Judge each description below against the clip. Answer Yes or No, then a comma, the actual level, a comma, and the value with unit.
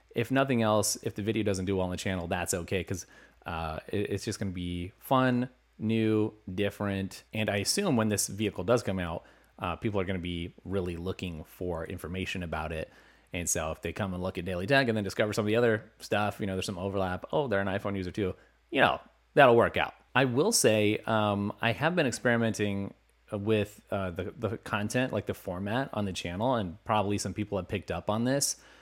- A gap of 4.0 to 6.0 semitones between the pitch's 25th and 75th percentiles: No, average, 2.8 semitones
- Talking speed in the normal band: No, fast, 225 wpm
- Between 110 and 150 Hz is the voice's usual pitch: No, low, 100 Hz